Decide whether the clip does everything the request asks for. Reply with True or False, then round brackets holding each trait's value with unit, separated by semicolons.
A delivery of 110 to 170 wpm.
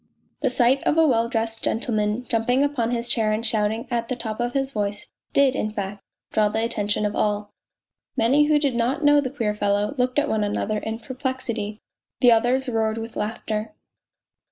False (190 wpm)